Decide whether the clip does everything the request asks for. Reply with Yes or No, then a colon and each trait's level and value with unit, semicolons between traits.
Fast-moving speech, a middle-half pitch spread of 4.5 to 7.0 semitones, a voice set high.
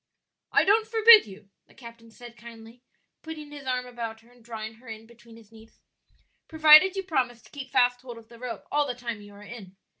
No: fast, 215 wpm; average, 3.9 semitones; high, 240 Hz